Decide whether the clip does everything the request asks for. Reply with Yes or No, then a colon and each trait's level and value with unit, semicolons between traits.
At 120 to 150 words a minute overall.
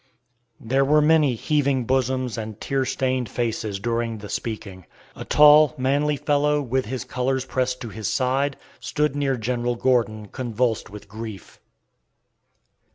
Yes: average, 140 wpm